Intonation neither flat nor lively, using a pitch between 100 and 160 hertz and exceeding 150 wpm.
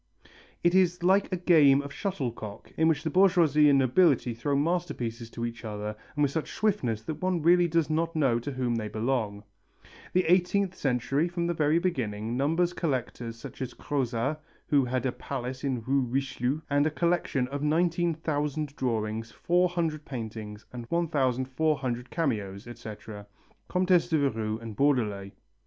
No: wide, 6.0 semitones; medium, 140 Hz; average, 160 wpm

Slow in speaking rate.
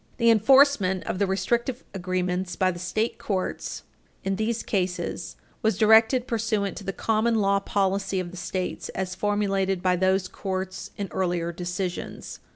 No: average, 155 wpm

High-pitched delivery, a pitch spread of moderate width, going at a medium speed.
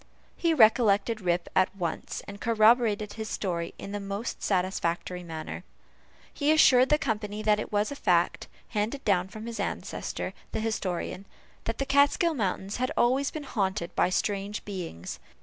Yes: high, 210 Hz; average, 4.0 semitones; average, 160 wpm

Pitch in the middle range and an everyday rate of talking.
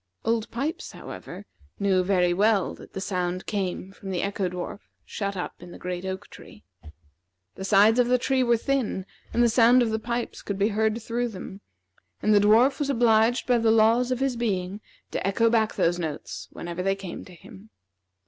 No: high, 210 Hz; average, 195 wpm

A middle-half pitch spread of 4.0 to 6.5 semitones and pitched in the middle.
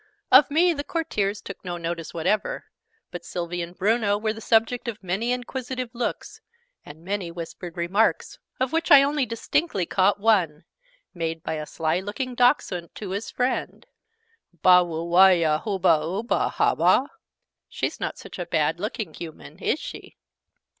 No: wide, 5.5 semitones; high, 195 Hz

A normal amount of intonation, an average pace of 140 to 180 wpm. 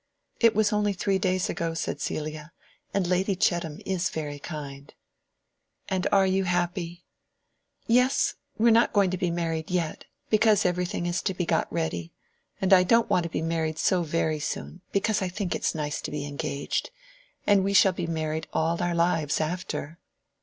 No: average, 3.2 semitones; average, 190 wpm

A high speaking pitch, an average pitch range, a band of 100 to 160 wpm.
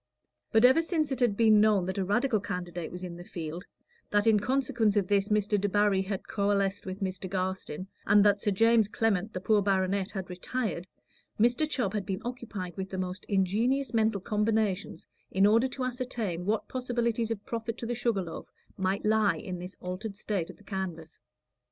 No: high, 205 Hz; average, 3.2 semitones; average, 190 wpm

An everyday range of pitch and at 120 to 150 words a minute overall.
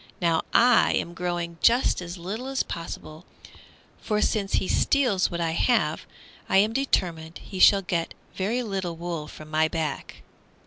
No: average, 4.2 semitones; average, 160 wpm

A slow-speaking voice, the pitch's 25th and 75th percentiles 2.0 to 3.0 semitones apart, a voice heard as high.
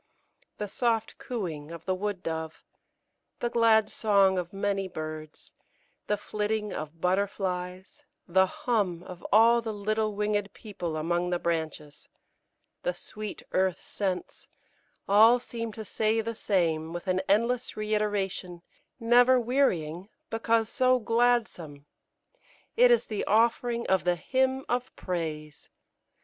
No: slow, 130 wpm; average, 4.4 semitones; high, 205 Hz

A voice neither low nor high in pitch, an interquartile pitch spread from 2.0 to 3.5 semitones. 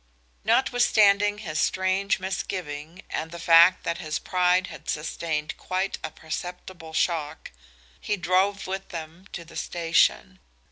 Yes: medium, 180 Hz; average, 2.8 semitones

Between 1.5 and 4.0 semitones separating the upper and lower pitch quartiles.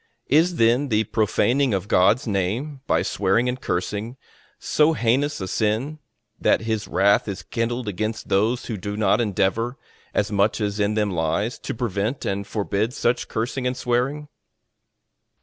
Yes: average, 3.6 semitones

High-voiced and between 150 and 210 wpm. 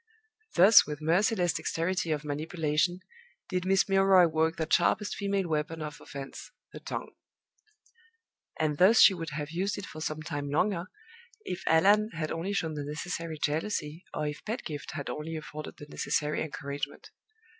No: medium, 160 Hz; average, 155 wpm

